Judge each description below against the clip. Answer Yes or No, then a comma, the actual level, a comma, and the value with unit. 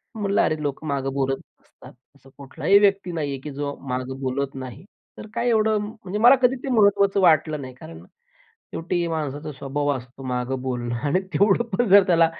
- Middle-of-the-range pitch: Yes, medium, 150 Hz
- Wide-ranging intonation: Yes, wide, 6.9 semitones